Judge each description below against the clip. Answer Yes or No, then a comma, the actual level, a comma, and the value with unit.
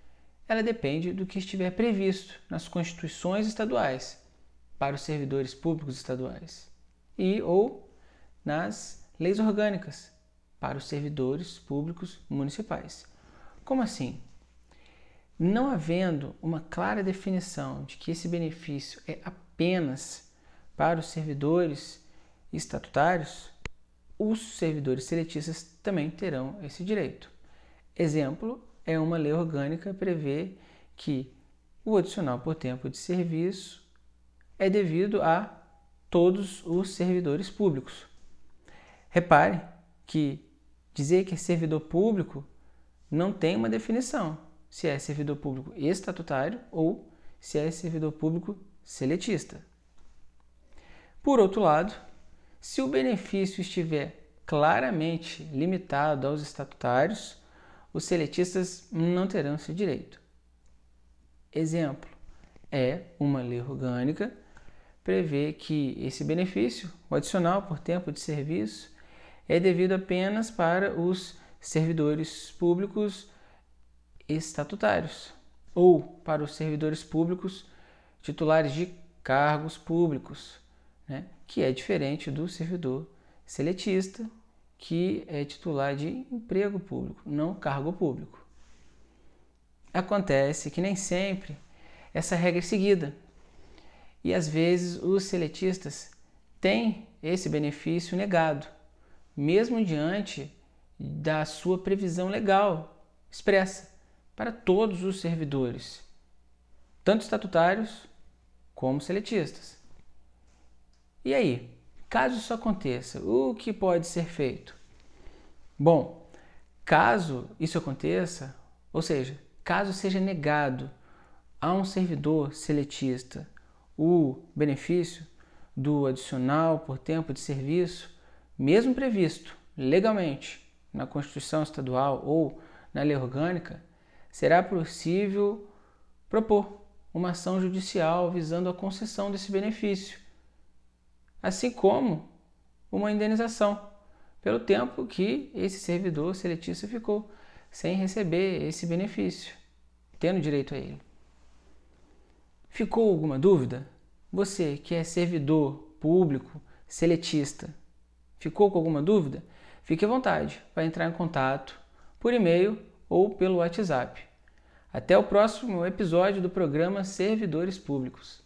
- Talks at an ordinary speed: No, slow, 105 wpm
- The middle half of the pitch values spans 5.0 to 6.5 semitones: Yes, wide, 5.6 semitones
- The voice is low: No, medium, 160 Hz